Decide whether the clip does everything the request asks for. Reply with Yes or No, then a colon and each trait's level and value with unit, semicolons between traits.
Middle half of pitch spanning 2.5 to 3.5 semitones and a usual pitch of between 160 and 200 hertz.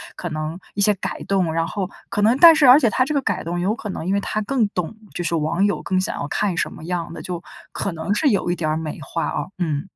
No: average, 4.1 semitones; medium, 185 Hz